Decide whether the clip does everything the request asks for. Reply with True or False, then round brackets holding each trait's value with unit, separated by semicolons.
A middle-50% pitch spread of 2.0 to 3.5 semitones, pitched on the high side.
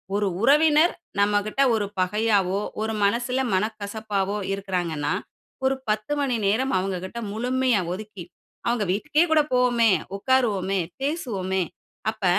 False (4.3 semitones; 215 Hz)